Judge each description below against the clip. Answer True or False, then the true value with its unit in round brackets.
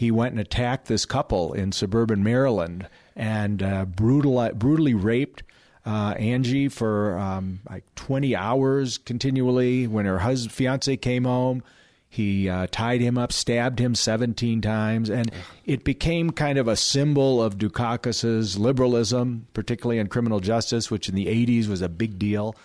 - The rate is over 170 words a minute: False (155 wpm)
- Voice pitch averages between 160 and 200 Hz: False (115 Hz)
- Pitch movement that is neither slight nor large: True (3.0 semitones)